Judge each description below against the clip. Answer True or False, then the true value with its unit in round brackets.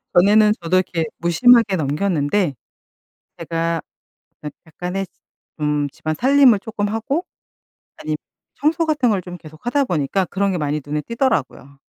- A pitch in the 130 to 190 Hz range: True (185 Hz)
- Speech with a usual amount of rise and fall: False (6.3 semitones)